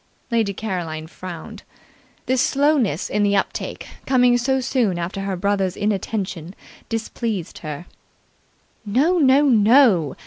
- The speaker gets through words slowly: Yes, slow, 115 wpm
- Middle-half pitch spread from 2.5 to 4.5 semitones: No, average, 5.2 semitones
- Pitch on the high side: Yes, high, 210 Hz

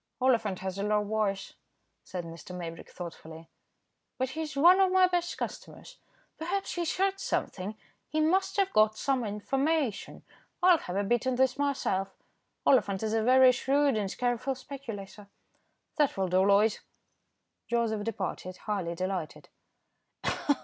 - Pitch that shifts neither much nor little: No, wide, 6.4 semitones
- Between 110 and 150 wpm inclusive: Yes, average, 140 wpm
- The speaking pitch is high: Yes, high, 225 Hz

